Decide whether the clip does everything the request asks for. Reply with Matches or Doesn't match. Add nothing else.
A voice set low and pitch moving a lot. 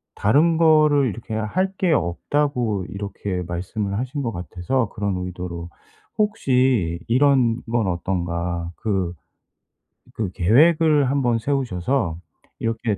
Matches